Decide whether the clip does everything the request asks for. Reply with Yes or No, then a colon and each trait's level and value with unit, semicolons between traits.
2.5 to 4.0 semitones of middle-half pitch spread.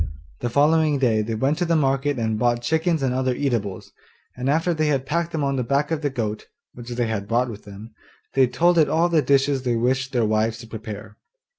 No: average, 4.4 semitones